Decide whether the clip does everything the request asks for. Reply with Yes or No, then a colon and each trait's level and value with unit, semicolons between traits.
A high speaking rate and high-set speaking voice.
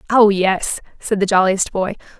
No: average, 165 wpm; high, 195 Hz